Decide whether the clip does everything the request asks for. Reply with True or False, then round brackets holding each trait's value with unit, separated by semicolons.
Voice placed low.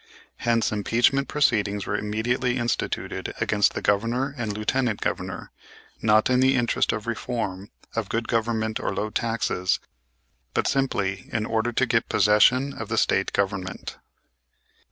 True (115 Hz)